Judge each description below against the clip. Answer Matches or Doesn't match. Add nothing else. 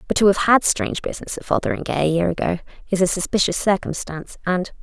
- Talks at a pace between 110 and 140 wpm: Doesn't match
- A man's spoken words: Doesn't match